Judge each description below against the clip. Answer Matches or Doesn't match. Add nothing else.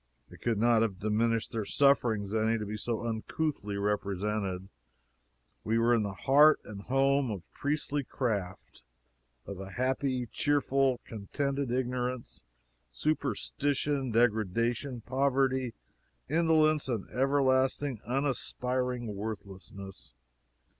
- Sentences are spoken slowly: Matches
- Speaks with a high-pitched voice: Doesn't match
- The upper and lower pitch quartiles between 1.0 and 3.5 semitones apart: Doesn't match